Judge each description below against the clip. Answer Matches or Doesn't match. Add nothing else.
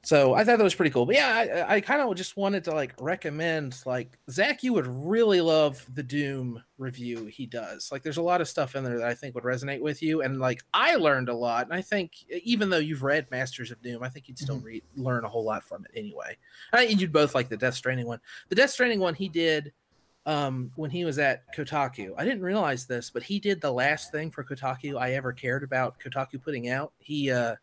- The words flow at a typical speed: Doesn't match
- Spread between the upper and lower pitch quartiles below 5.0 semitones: Doesn't match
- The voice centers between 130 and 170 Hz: Matches